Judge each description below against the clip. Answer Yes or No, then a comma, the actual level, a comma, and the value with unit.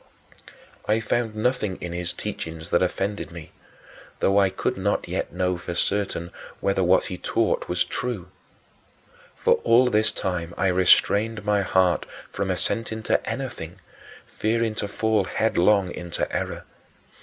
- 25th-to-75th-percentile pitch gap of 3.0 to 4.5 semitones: Yes, average, 3.4 semitones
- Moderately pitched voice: No, very low, 95 Hz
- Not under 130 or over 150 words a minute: Yes, average, 145 wpm